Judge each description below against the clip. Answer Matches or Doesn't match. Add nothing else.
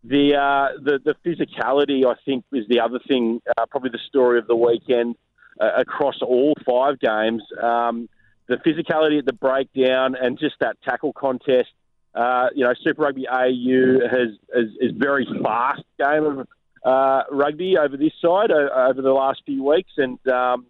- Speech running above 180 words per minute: Doesn't match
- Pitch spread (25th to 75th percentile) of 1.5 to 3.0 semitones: Matches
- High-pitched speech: Doesn't match